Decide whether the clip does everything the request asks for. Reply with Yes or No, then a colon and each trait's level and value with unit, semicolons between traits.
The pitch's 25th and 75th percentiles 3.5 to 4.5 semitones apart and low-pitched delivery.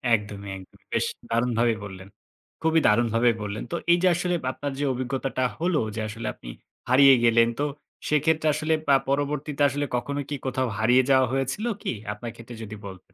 Yes: average, 4.2 semitones; low, 130 Hz